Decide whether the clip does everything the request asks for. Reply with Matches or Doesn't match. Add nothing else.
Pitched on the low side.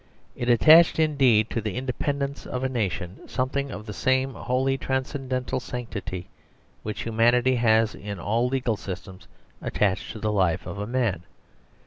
Matches